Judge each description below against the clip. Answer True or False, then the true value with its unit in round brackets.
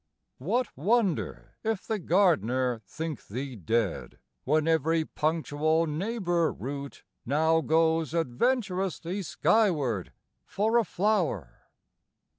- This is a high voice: False (160 Hz)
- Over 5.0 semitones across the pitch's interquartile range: True (5.6 semitones)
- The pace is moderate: False (95 wpm)